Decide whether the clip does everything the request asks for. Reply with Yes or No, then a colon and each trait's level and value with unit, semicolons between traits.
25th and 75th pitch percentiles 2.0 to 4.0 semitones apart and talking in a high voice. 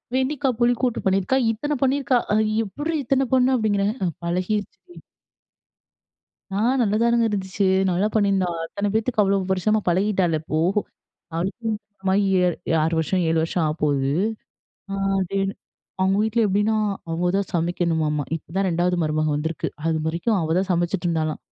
No: average, 4.4 semitones; high, 195 Hz